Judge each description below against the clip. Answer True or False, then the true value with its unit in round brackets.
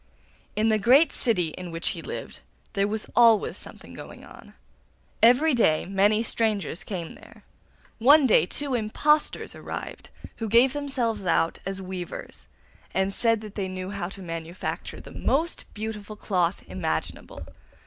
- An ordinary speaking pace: True (150 wpm)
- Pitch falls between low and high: False (210 Hz)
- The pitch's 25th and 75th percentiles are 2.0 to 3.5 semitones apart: False (4.0 semitones)